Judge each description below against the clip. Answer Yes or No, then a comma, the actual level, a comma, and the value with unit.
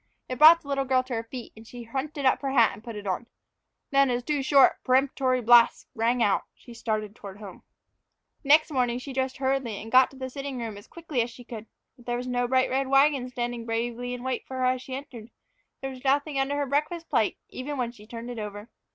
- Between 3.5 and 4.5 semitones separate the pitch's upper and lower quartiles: No, narrow, 2.6 semitones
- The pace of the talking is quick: Yes, fast, 235 wpm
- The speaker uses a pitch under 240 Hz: No, very high, 255 Hz